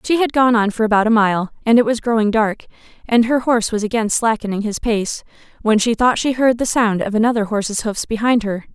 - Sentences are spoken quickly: Yes, fast, 235 wpm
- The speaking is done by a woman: Yes, female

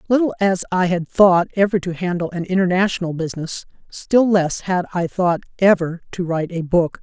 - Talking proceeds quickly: No, average, 180 wpm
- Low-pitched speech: No, medium, 180 Hz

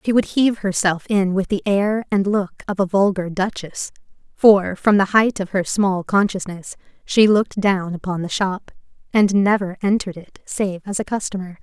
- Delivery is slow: No, average, 185 wpm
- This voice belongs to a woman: Yes, female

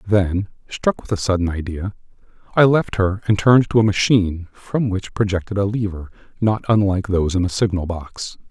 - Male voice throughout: Yes, male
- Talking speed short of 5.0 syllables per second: No, 5.4 syllables/s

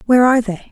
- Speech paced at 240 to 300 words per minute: Yes, fast, 255 wpm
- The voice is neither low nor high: No, high, 235 Hz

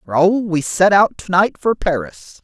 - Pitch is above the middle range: No, medium, 170 Hz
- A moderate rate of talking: Yes, average, 195 wpm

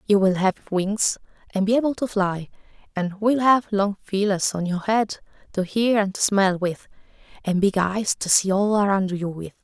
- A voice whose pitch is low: No, high, 200 Hz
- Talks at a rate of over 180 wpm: Yes, average, 200 wpm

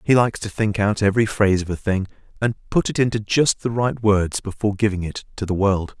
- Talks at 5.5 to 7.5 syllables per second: Yes, 5.9 syllables/s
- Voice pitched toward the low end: Yes, low, 105 Hz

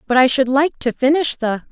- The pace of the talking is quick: Yes, fast, 245 wpm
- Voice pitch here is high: Yes, very high, 265 Hz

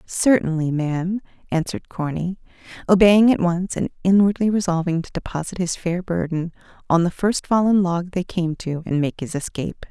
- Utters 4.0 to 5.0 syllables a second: No, 5.2 syllables/s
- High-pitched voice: No, medium, 180 Hz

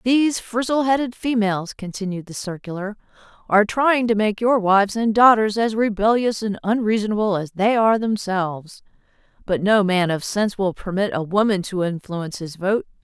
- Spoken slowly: No, average, 165 wpm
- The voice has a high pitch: Yes, high, 210 Hz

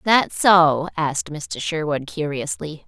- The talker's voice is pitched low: No, medium, 160 Hz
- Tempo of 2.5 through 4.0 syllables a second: Yes, 3.8 syllables/s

